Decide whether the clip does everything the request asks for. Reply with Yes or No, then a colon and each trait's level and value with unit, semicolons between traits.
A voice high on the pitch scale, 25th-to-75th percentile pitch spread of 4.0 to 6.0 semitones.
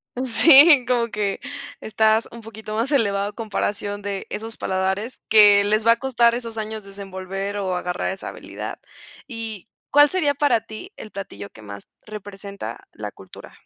No: high, 215 Hz; average, 2.8 semitones